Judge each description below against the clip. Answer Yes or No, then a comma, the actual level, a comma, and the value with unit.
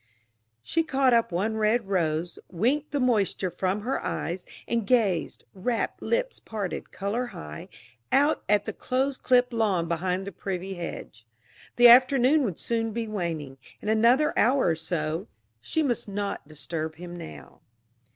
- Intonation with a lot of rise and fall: Yes, wide, 6.1 semitones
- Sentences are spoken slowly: No, average, 150 wpm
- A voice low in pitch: No, high, 205 Hz